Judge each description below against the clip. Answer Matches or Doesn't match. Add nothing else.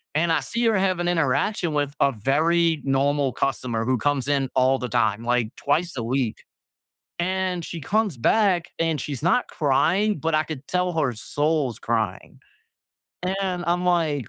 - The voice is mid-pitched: Matches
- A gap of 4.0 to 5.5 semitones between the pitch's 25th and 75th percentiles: Matches